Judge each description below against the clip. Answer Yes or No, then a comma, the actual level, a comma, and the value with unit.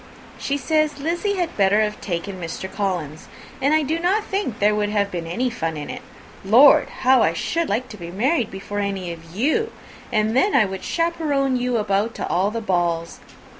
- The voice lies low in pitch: No, high, 215 Hz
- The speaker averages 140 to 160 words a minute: No, average, 200 wpm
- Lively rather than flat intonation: Yes, wide, 7.0 semitones